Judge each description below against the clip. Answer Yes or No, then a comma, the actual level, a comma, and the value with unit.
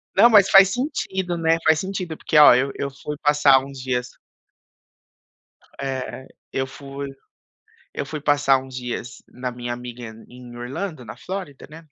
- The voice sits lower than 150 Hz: Yes, medium, 140 Hz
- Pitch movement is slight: No, average, 4.3 semitones